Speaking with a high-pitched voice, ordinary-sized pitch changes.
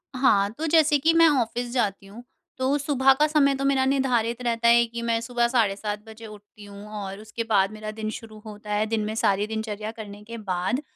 Yes: high, 225 Hz; average, 3.4 semitones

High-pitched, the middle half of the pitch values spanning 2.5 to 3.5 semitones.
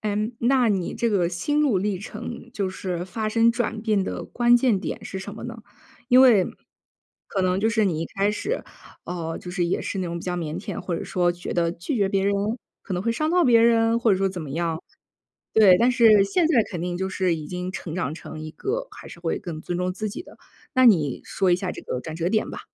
No: high, 195 Hz; average, 4.5 semitones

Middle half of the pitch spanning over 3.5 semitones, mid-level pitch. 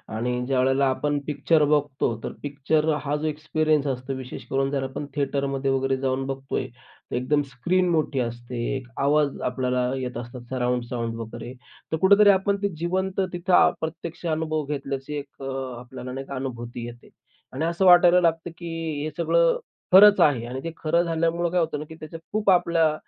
Yes: average, 4.1 semitones; medium, 145 Hz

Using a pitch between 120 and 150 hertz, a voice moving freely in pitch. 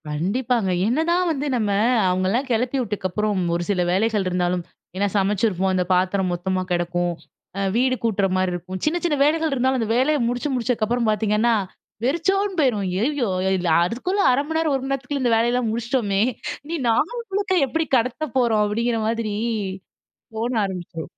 No: high, 230 Hz; wide, 5.8 semitones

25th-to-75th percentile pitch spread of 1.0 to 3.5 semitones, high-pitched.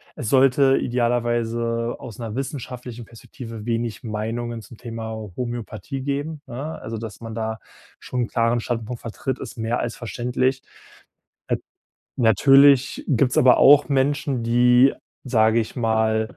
No: narrow, 2.4 semitones; low, 120 Hz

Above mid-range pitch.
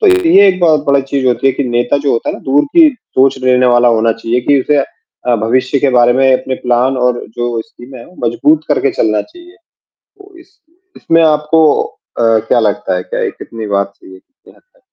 No: low, 130 Hz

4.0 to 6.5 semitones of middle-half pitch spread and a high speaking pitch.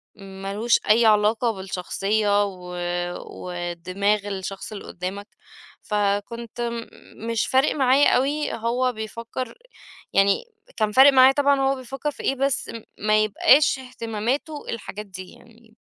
Yes: average, 4.4 semitones; high, 220 Hz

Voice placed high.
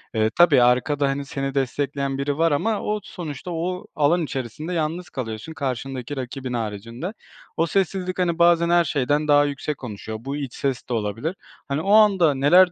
No: medium, 145 Hz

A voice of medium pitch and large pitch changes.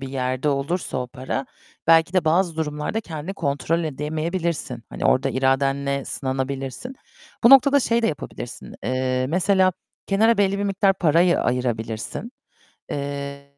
Yes: medium, 150 Hz; wide, 5.7 semitones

